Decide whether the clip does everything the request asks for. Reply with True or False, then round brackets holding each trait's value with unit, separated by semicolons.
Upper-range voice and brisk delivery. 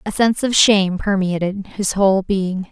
False (195 Hz; 175 wpm)